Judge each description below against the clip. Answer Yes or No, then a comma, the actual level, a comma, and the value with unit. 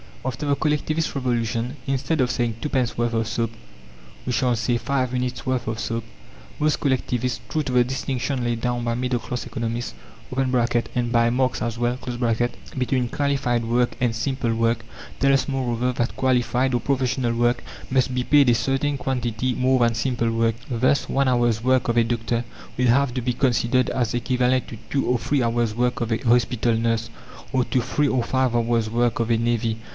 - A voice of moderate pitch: No, low, 125 Hz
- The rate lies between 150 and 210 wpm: Yes, average, 190 wpm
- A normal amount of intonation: No, narrow, 1.8 semitones